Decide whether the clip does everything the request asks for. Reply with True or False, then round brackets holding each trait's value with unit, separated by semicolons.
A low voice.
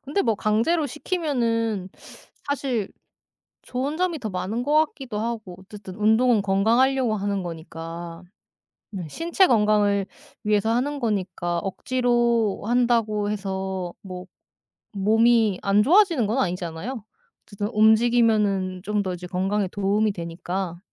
False (210 Hz)